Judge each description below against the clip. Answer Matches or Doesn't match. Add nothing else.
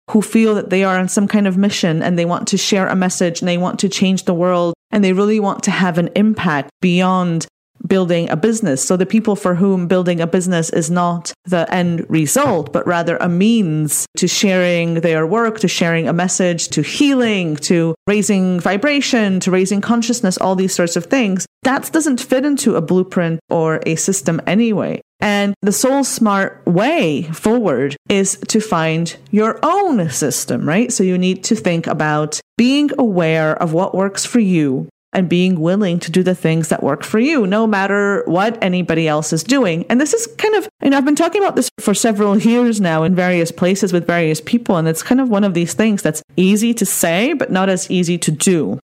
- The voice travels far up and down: Doesn't match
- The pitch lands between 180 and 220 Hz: Matches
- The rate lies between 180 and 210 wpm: Matches